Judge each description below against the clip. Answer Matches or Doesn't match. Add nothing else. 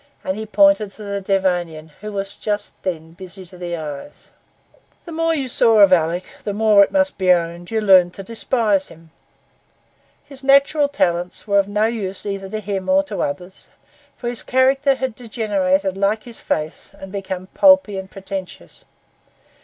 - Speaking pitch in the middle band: Doesn't match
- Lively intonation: Doesn't match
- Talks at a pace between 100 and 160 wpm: Doesn't match